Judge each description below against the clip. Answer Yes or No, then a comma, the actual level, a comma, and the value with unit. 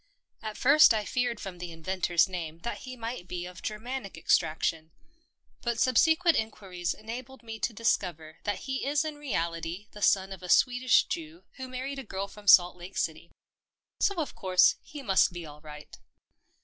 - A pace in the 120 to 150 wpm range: No, average, 175 wpm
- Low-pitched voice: No, high, 205 Hz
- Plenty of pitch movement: Yes, wide, 6.4 semitones